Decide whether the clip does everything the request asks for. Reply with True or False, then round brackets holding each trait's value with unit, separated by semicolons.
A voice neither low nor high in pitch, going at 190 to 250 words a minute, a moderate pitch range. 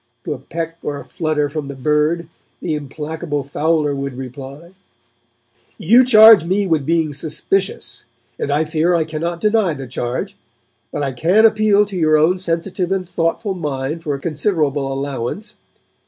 False (160 Hz; 160 wpm; 4.1 semitones)